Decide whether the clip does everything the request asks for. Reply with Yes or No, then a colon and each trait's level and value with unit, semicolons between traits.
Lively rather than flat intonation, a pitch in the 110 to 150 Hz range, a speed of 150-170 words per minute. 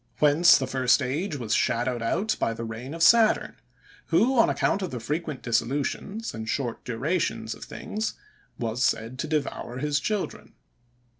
Yes: wide, 6.0 semitones; medium, 140 Hz; average, 160 wpm